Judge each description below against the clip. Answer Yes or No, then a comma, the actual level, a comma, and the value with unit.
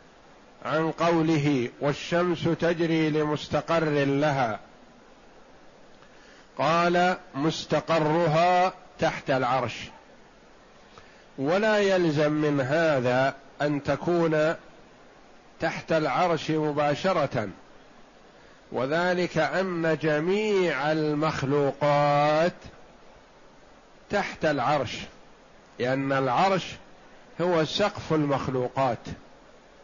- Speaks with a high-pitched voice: No, medium, 155 Hz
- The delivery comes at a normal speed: No, slow, 60 wpm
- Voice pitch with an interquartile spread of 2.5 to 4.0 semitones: Yes, average, 2.8 semitones